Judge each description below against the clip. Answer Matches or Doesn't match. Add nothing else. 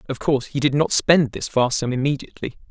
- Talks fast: Matches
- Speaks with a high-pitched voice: Doesn't match